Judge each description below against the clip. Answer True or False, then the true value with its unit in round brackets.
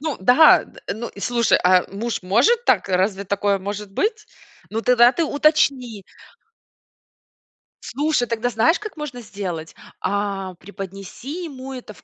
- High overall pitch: True (230 Hz)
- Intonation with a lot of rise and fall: True (6.0 semitones)